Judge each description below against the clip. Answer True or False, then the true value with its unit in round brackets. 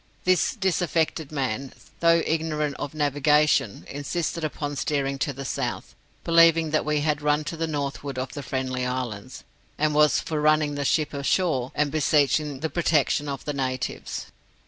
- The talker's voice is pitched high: False (150 Hz)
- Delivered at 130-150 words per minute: False (160 wpm)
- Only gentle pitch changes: True (2.2 semitones)